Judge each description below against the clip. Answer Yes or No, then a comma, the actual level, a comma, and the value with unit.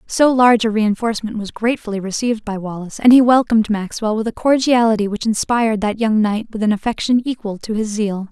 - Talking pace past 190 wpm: Yes, average, 200 wpm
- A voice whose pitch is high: Yes, high, 220 Hz